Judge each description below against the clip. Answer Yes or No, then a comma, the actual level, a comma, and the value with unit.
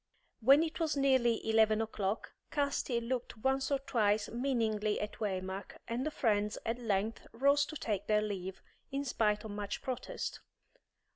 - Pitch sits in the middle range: No, high, 230 Hz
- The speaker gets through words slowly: No, average, 155 wpm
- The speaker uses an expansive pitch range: No, average, 4.2 semitones